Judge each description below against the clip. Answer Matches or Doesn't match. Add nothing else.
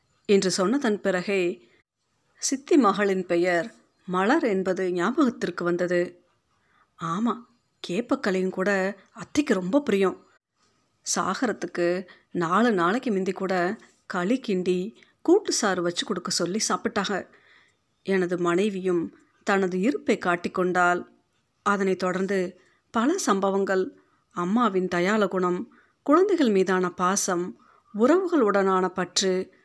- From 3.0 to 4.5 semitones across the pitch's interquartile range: Matches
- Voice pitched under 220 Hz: Matches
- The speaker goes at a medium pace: Matches